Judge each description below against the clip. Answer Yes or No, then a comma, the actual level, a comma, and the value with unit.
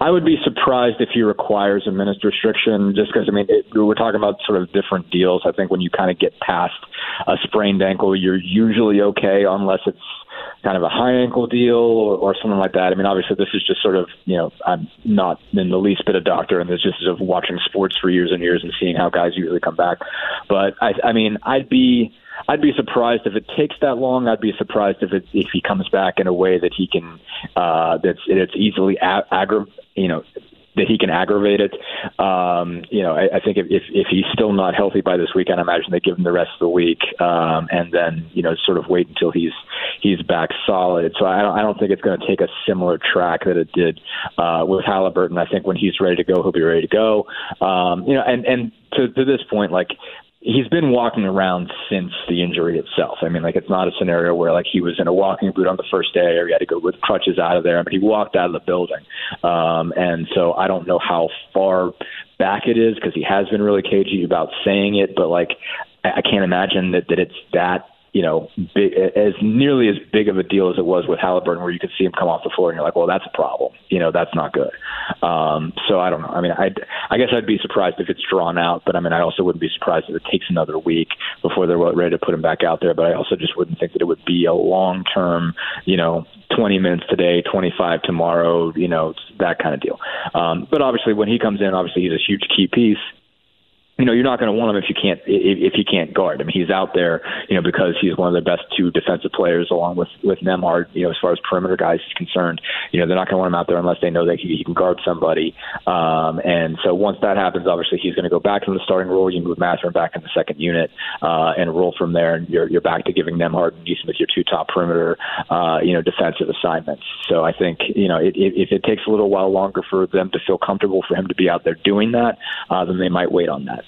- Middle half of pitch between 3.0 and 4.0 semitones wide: Yes, average, 3.3 semitones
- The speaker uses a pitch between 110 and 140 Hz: No, very low, 95 Hz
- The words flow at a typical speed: No, fast, 260 wpm